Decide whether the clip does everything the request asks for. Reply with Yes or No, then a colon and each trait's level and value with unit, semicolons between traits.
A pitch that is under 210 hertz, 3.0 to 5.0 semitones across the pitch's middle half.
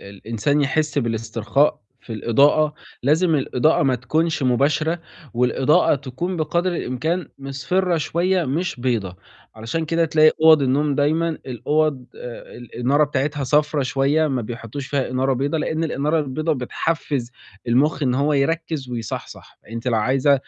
Yes: medium, 140 Hz; average, 3.7 semitones